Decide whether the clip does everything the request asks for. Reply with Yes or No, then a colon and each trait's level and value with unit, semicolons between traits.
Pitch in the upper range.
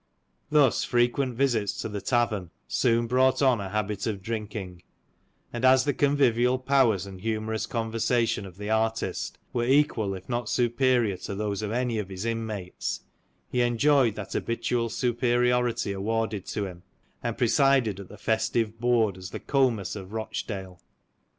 No: low, 115 Hz